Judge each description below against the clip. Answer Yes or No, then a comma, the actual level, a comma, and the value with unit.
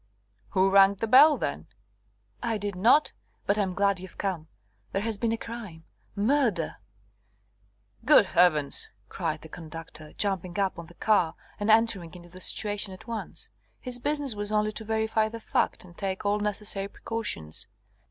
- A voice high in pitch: Yes, high, 200 Hz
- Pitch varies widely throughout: No, average, 3.6 semitones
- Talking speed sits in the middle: Yes, average, 165 wpm